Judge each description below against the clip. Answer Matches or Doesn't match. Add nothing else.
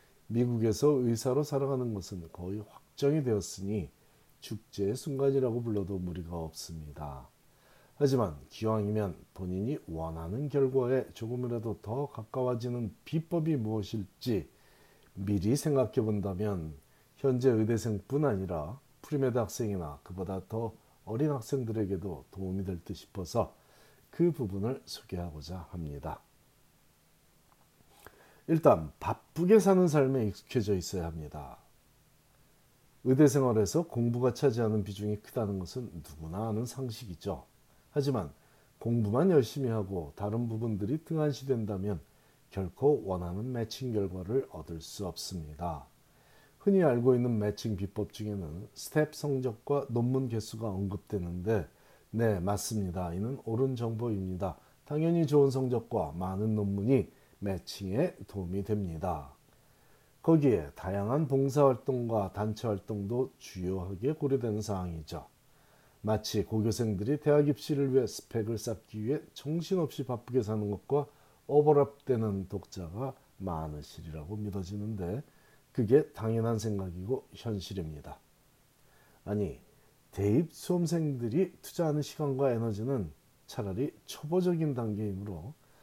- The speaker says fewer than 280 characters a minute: Doesn't match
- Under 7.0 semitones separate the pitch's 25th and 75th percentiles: Matches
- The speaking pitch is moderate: Doesn't match